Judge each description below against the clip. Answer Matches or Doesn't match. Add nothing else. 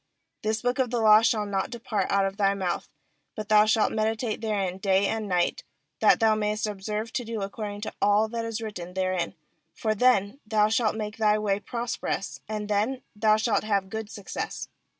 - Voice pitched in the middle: Doesn't match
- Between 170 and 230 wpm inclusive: Matches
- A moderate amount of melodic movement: Doesn't match